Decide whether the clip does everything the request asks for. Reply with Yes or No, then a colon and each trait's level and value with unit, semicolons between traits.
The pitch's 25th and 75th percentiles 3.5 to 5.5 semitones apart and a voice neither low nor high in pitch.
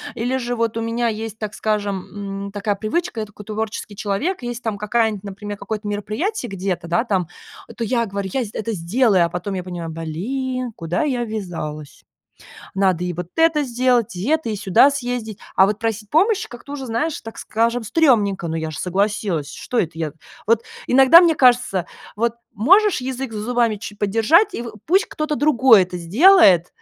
No: average, 4.2 semitones; high, 220 Hz